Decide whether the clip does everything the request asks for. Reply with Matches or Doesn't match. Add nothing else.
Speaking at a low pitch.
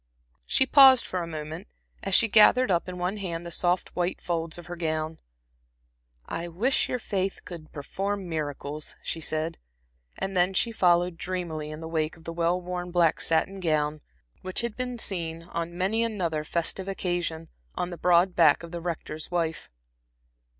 Doesn't match